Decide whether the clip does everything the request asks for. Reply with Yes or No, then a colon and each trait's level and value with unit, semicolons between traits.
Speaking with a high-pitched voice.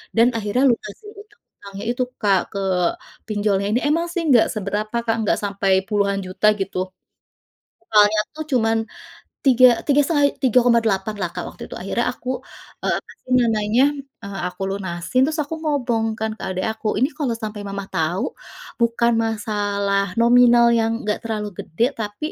Yes: high, 220 Hz